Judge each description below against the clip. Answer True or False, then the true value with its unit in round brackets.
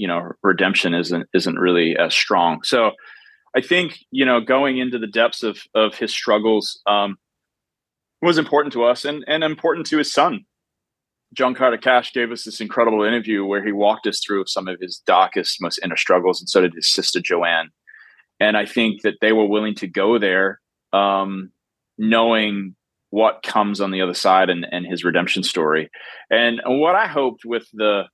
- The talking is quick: False (185 wpm)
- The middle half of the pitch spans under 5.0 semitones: True (4.2 semitones)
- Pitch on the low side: True (105 Hz)